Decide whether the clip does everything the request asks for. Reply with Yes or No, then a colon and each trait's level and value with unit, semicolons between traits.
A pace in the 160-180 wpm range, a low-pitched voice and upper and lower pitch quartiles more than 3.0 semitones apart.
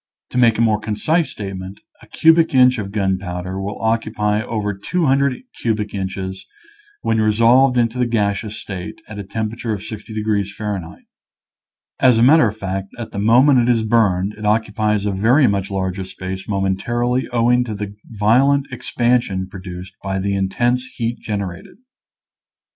Yes: average, 165 wpm; low, 105 Hz; average, 3.4 semitones